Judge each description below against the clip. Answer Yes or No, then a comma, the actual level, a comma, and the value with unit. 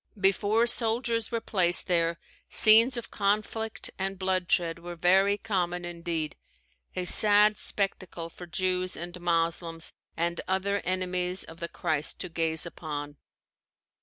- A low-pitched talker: No, medium, 180 Hz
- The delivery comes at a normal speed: No, slow, 130 wpm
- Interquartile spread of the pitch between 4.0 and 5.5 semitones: No, average, 3.1 semitones